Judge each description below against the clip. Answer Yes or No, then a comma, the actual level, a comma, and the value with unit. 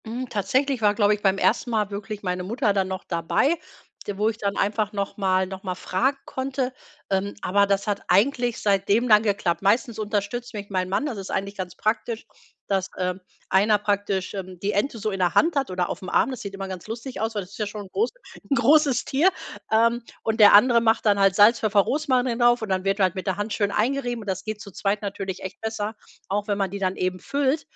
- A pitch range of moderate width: Yes, average, 3.1 semitones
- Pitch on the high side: Yes, high, 205 Hz